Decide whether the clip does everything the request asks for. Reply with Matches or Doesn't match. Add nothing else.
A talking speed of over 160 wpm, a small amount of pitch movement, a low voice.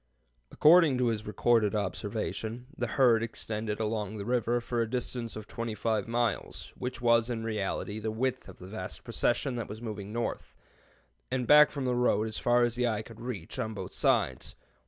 Matches